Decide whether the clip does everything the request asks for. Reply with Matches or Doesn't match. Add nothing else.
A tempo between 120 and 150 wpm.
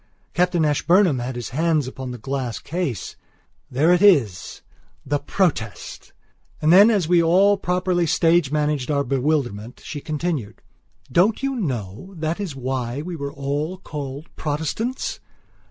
Matches